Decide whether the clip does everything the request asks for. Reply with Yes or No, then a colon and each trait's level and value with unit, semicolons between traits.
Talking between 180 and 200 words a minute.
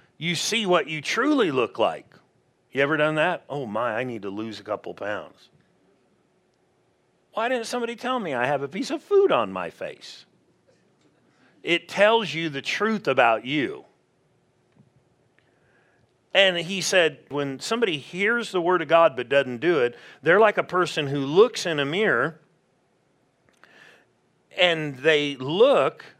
No: average, 155 wpm